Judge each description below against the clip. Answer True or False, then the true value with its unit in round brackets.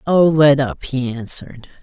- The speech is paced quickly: False (165 wpm)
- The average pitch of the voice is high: False (140 Hz)